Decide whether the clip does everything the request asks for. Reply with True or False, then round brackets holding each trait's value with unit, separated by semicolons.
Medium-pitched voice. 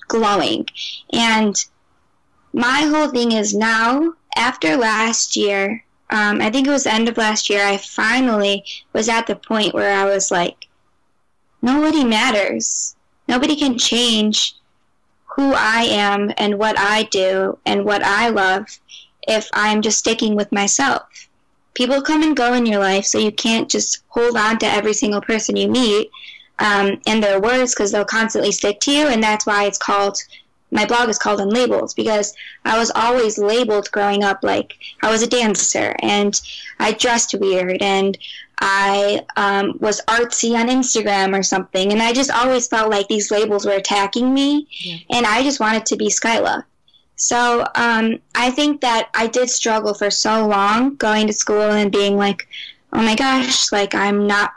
False (220 Hz)